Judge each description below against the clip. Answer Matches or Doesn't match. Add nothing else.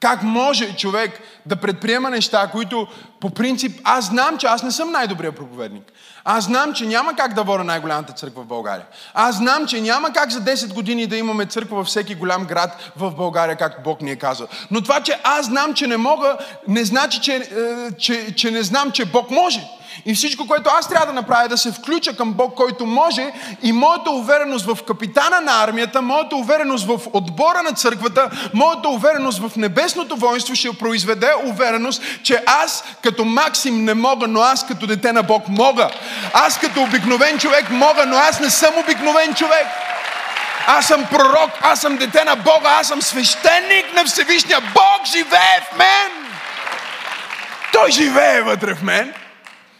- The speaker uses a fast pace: Matches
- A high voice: Matches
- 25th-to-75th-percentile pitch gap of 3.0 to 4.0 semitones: Doesn't match